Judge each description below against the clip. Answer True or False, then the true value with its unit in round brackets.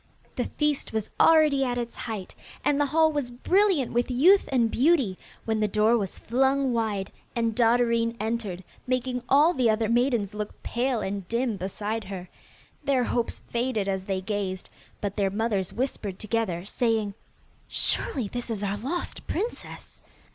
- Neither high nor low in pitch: False (230 Hz)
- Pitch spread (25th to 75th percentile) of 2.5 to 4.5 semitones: True (4.1 semitones)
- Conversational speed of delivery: True (160 wpm)